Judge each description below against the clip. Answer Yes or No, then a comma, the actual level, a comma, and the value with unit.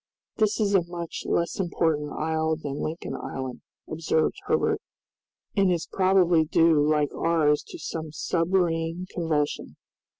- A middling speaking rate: No, slow, 130 wpm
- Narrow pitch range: Yes, narrow, 2.3 semitones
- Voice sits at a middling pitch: Yes, medium, 165 Hz